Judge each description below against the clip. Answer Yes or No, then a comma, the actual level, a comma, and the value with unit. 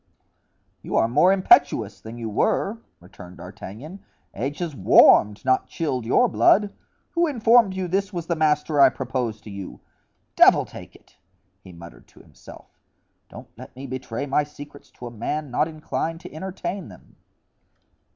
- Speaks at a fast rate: No, average, 160 wpm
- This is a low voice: No, medium, 145 Hz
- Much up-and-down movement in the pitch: Yes, wide, 7.6 semitones